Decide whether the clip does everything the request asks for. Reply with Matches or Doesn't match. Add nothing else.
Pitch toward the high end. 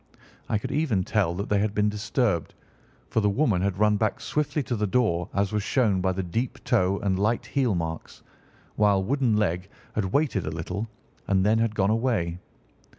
Doesn't match